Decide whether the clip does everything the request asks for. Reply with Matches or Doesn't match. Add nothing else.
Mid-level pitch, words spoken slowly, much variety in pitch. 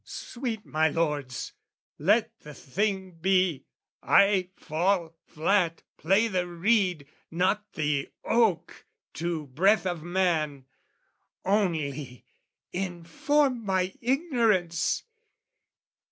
Doesn't match